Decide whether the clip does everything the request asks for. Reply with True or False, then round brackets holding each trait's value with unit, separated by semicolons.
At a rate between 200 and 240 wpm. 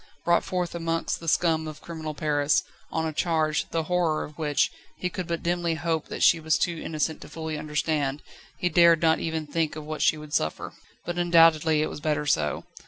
True (205 wpm)